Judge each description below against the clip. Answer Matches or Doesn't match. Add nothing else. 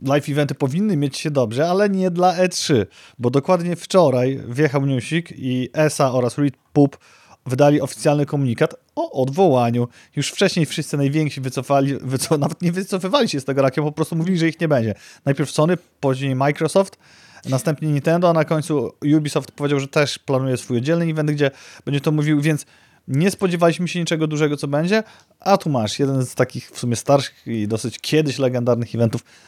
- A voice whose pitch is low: Doesn't match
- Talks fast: Matches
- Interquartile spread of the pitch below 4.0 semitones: Matches